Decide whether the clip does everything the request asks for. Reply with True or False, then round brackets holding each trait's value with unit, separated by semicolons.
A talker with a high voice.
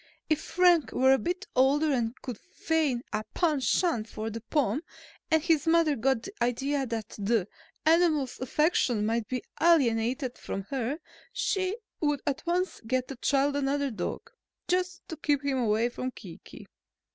True (275 Hz)